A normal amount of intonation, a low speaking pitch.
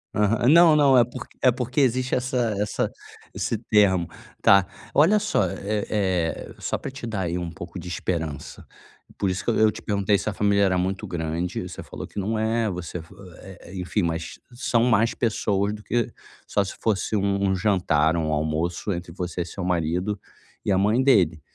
Yes: average, 4.3 semitones; low, 100 Hz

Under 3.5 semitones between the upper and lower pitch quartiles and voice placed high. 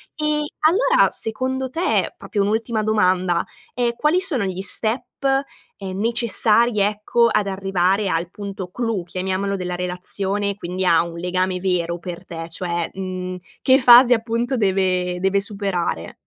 No: average, 4.1 semitones; high, 195 Hz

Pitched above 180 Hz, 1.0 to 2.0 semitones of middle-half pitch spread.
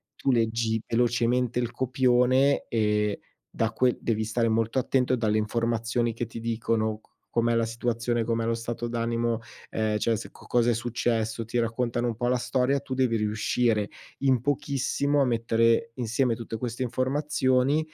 No: low, 115 Hz; narrow, 1.7 semitones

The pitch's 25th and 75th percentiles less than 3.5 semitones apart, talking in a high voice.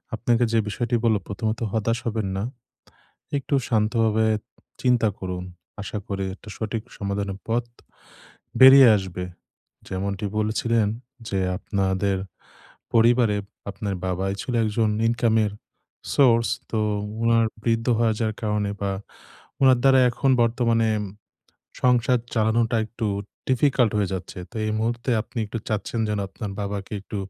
No: narrow, 2.5 semitones; low, 110 Hz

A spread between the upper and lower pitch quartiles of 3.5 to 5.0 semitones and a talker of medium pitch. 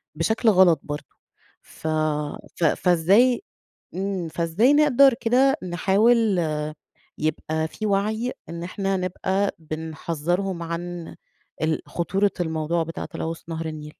Yes: average, 4.1 semitones; medium, 175 Hz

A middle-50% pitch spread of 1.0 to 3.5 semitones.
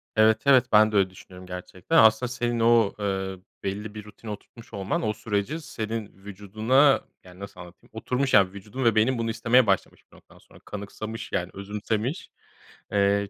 Yes: average, 2.7 semitones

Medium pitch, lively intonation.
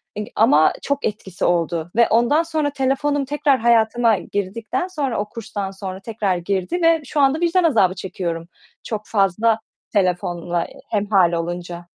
No: high, 210 Hz; wide, 6.8 semitones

